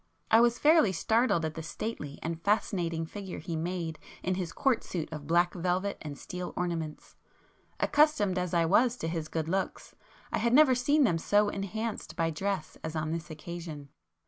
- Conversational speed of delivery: Yes, average, 180 wpm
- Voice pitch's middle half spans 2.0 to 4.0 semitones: No, average, 4.5 semitones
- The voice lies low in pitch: No, medium, 180 Hz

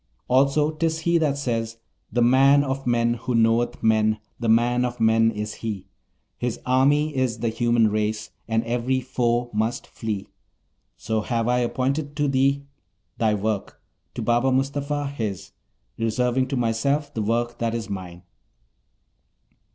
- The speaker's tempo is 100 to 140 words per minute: No, average, 150 wpm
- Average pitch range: Yes, average, 3.2 semitones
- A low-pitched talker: Yes, low, 120 Hz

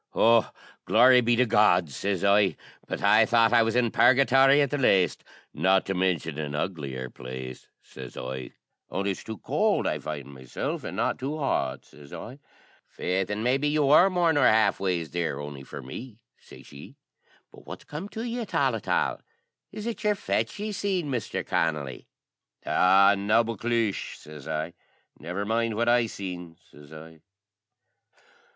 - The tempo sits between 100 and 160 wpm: No, average, 170 wpm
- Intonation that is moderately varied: No, wide, 8.1 semitones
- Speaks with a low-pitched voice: Yes, low, 100 Hz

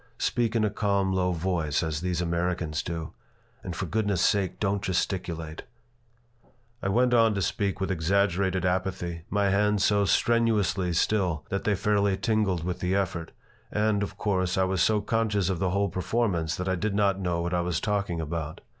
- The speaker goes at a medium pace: Yes, average, 180 wpm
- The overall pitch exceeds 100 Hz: No, very low, 95 Hz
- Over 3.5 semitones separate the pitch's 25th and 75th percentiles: No, average, 2.7 semitones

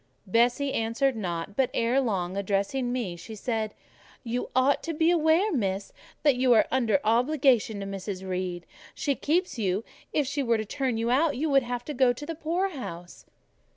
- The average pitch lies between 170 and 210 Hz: No, high, 245 Hz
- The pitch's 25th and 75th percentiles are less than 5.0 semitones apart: No, wide, 5.6 semitones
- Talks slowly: No, average, 185 wpm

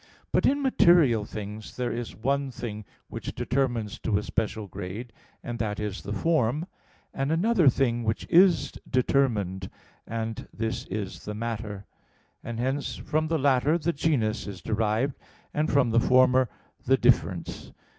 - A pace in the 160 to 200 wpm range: No, average, 150 wpm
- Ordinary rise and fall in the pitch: Yes, average, 4.6 semitones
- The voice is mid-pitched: No, low, 120 Hz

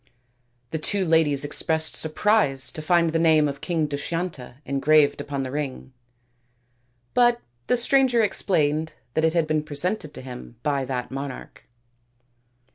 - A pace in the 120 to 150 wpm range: Yes, average, 145 wpm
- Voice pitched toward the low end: No, medium, 155 Hz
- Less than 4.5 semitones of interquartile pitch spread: Yes, average, 3.3 semitones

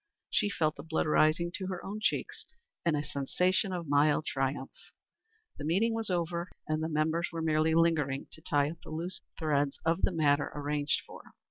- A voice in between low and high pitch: Yes, medium, 160 Hz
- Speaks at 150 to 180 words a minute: No, average, 190 wpm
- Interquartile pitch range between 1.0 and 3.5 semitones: Yes, average, 2.7 semitones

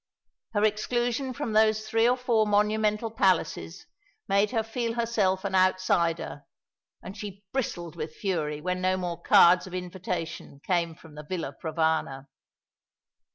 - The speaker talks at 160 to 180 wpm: No, average, 140 wpm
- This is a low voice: No, high, 190 Hz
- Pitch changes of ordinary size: Yes, average, 4.3 semitones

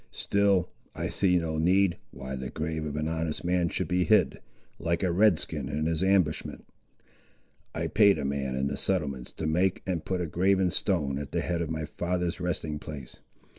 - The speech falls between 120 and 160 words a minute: No, average, 195 wpm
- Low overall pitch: Yes, very low, 85 Hz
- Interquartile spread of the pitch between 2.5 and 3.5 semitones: Yes, average, 3.1 semitones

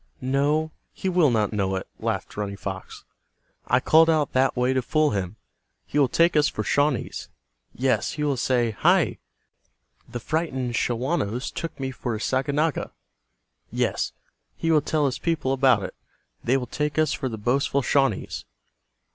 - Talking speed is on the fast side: No, average, 165 wpm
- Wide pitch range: No, average, 3.9 semitones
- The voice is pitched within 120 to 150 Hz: Yes, low, 135 Hz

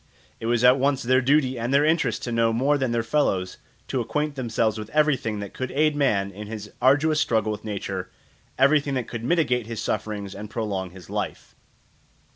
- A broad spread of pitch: No, average, 4.6 semitones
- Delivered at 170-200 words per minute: Yes, average, 195 wpm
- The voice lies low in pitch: Yes, low, 120 Hz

